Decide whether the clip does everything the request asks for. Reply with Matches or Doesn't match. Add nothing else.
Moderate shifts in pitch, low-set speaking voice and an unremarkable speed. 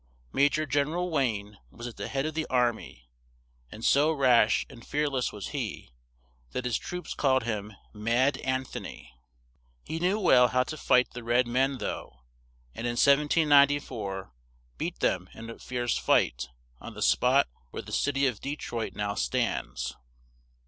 Matches